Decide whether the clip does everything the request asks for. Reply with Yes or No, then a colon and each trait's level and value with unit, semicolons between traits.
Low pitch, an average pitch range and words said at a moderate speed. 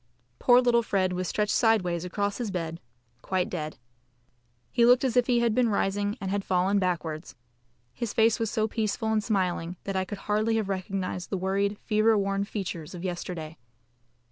No: high, 200 Hz; average, 3.3 semitones; average, 180 wpm